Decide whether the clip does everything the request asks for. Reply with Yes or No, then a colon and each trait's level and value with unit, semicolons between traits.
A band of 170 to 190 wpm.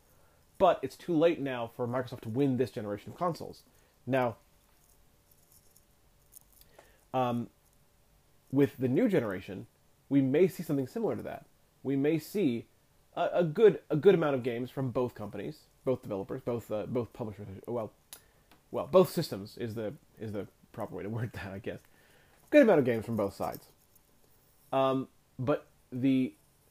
No: average, 160 wpm